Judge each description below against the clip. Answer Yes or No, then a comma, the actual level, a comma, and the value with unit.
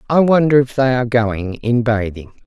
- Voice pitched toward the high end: No, low, 120 Hz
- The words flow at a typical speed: Yes, average, 195 wpm